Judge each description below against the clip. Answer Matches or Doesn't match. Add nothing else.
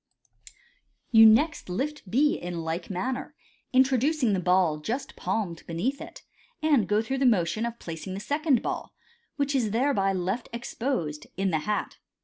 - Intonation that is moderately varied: Doesn't match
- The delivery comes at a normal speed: Matches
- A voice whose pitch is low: Doesn't match